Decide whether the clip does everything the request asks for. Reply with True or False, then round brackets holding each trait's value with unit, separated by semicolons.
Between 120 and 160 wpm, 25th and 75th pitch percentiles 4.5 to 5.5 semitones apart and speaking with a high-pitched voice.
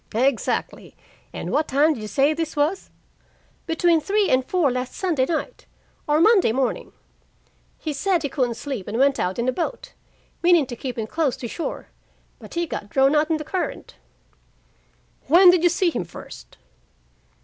False (175 wpm; 5.0 semitones; 300 Hz)